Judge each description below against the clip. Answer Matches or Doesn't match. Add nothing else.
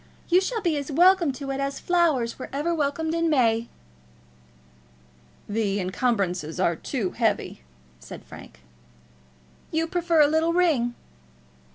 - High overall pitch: Matches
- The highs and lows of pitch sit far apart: Matches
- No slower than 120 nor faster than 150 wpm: Matches